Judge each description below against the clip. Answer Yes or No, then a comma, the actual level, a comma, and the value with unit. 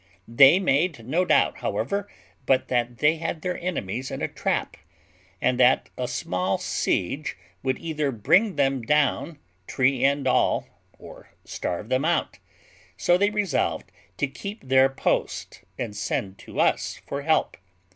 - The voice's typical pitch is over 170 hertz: No, low, 135 Hz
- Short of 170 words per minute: Yes, average, 145 wpm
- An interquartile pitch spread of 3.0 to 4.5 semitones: No, average, 4.9 semitones